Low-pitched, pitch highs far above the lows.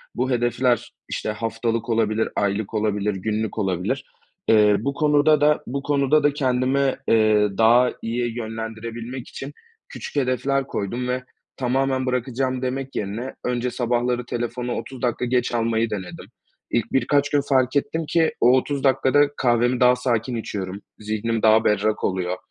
No: low, 120 Hz; average, 2.9 semitones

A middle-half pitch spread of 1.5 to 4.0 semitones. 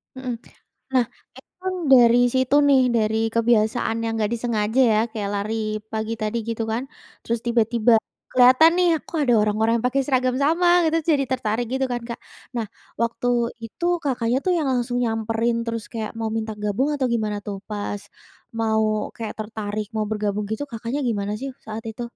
Yes: average, 2.7 semitones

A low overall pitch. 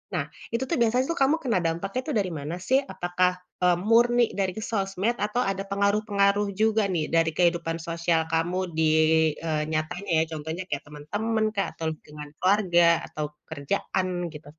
No: medium, 185 Hz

